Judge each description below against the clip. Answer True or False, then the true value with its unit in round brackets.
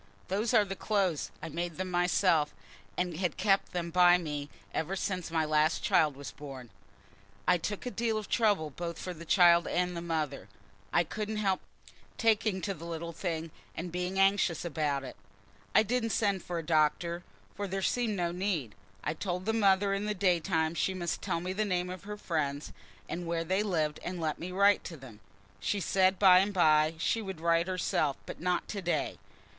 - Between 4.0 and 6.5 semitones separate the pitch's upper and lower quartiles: False (3.2 semitones)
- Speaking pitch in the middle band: True (180 Hz)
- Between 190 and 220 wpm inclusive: True (200 wpm)